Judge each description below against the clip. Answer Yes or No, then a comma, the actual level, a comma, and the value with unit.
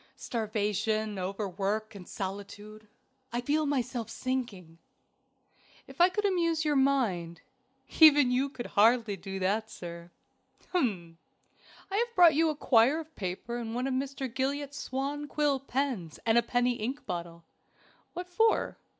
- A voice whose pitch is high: Yes, high, 240 Hz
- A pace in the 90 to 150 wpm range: Yes, average, 140 wpm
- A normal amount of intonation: No, wide, 5.9 semitones